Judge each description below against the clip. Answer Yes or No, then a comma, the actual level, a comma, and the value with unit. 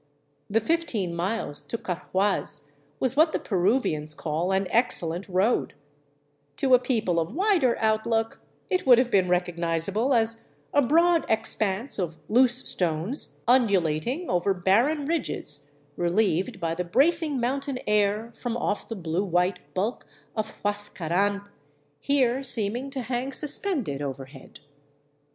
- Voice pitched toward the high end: Yes, high, 215 Hz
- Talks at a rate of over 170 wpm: No, slow, 135 wpm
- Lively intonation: Yes, wide, 6.2 semitones